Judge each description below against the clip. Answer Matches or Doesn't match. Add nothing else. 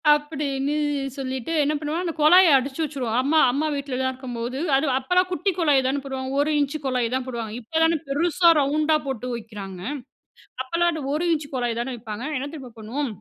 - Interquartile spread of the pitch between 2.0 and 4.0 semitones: Matches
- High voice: Matches